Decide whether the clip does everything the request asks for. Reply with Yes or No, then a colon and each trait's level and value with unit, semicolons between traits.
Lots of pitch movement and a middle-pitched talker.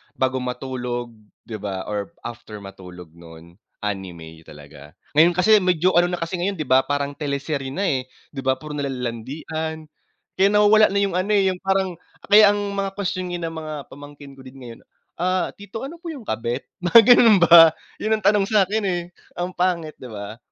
Yes: wide, 7.7 semitones; medium, 155 Hz